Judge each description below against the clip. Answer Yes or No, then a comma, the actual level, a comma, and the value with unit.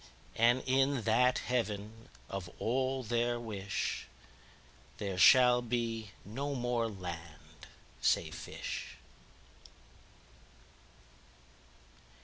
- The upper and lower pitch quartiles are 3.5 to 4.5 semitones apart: Yes, average, 4.1 semitones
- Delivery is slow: Yes, slow, 75 wpm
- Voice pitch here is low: Yes, low, 115 Hz